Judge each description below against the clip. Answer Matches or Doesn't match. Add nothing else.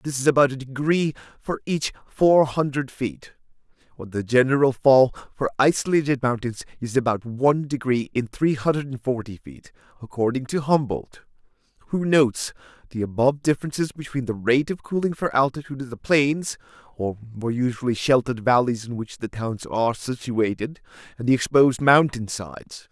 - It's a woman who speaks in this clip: Doesn't match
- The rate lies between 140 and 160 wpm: Matches